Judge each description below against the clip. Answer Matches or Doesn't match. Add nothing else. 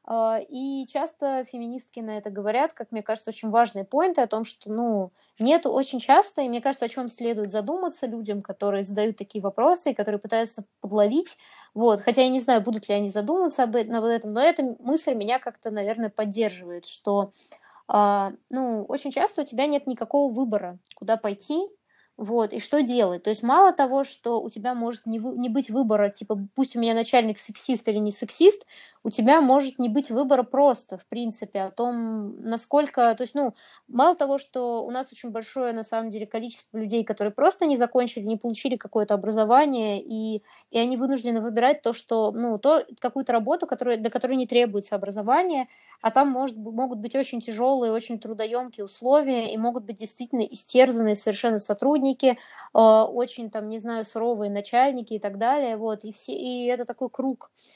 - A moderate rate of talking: Doesn't match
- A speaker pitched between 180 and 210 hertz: Doesn't match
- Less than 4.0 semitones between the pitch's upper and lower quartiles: Matches